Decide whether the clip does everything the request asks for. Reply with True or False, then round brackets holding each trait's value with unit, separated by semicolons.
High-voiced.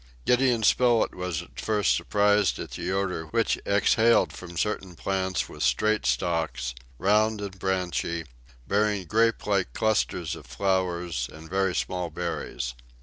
False (95 Hz)